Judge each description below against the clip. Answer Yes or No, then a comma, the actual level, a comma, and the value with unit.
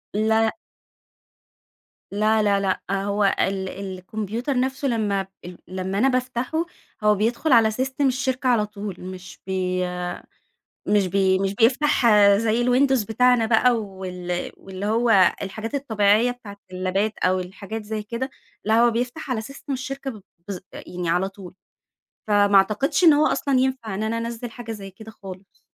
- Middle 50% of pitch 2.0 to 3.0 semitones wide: No, average, 4.1 semitones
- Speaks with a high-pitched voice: Yes, high, 215 Hz